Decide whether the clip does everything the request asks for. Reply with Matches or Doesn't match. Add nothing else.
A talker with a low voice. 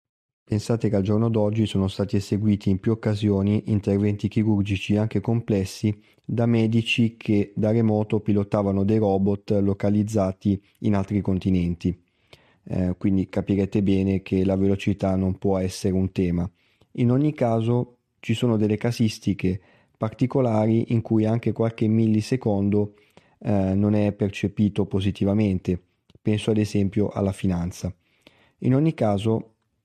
Matches